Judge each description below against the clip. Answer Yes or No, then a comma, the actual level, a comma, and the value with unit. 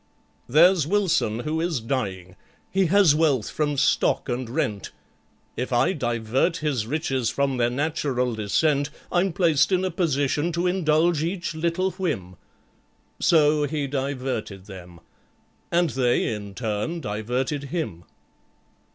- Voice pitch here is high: No, medium, 145 Hz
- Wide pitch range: Yes, wide, 5.7 semitones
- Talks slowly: Yes, slow, 125 wpm